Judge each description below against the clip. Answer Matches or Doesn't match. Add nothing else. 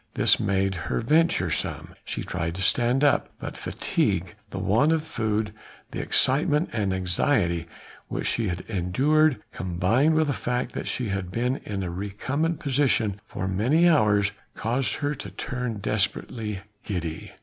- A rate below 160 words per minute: Matches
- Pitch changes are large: Matches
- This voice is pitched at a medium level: Doesn't match